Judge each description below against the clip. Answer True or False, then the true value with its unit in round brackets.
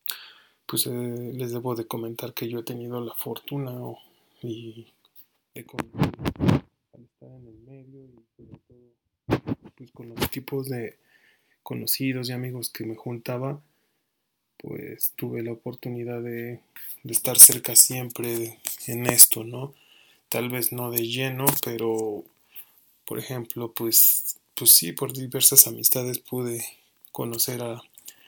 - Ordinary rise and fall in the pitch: False (1.6 semitones)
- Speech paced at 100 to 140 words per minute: True (135 wpm)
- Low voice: True (120 Hz)